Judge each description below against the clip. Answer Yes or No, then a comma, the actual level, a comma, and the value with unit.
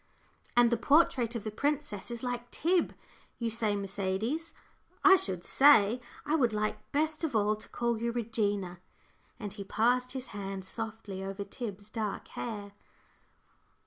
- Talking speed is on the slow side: No, average, 150 wpm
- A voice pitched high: Yes, high, 225 Hz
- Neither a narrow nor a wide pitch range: Yes, average, 3.6 semitones